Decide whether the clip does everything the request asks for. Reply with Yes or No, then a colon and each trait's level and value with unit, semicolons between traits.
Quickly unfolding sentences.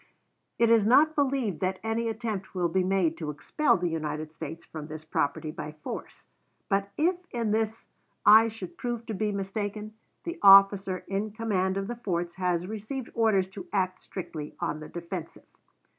No: average, 175 wpm